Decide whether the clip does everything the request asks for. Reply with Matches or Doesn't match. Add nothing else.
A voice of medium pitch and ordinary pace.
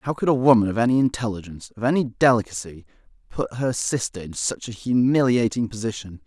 Doesn't match